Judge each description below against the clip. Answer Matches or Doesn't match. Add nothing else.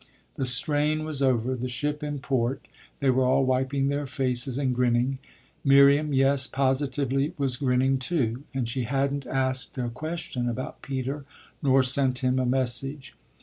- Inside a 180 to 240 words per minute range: Doesn't match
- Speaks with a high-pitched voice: Doesn't match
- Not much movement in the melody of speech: Matches